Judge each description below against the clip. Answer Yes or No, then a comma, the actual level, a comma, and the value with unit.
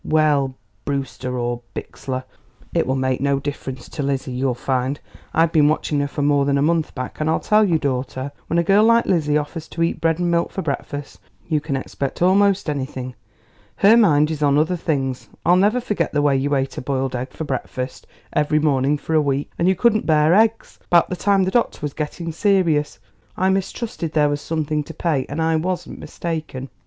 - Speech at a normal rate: No, fast, 210 wpm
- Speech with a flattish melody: No, average, 3.7 semitones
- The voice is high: No, medium, 150 Hz